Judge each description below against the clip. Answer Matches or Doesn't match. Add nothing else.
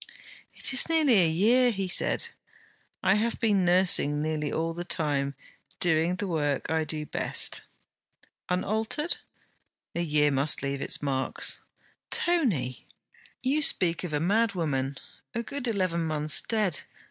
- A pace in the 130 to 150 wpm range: Matches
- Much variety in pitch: Matches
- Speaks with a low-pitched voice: Doesn't match